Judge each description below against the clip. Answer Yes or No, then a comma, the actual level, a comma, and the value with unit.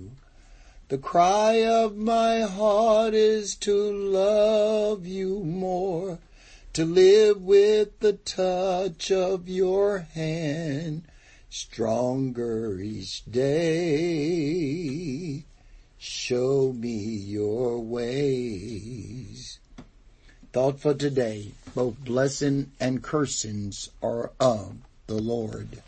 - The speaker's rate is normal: No, slow, 85 wpm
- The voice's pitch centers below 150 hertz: Yes, medium, 140 Hz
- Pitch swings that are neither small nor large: No, wide, 8.3 semitones